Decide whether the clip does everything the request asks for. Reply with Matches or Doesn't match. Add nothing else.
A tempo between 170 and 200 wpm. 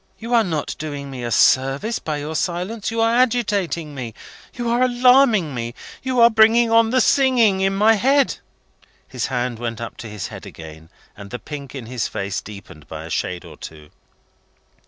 Matches